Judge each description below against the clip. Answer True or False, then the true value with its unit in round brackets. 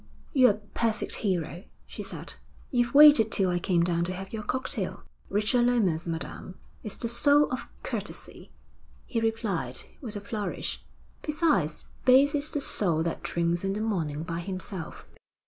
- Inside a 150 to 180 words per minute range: True (160 wpm)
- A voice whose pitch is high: True (205 Hz)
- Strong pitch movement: True (5.7 semitones)